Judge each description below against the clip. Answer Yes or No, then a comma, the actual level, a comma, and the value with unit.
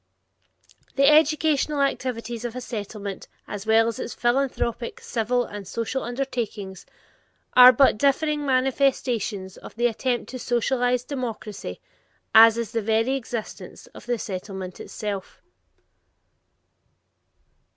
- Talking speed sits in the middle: No, slow, 110 wpm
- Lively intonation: No, average, 3.3 semitones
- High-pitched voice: Yes, high, 240 Hz